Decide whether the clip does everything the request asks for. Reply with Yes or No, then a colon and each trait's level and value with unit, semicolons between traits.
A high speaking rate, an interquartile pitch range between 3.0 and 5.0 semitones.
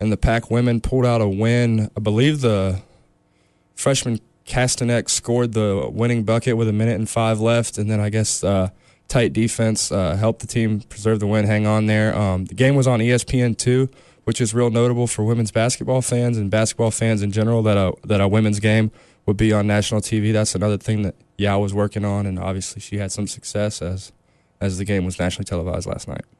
No: fast, 215 wpm; narrow, 2.4 semitones